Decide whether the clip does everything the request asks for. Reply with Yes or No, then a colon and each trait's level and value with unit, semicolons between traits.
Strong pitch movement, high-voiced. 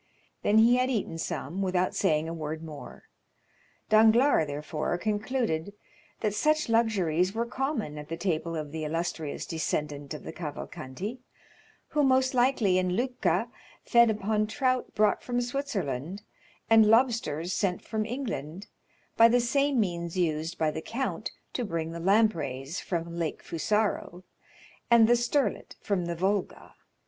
Yes: wide, 6.3 semitones; high, 195 Hz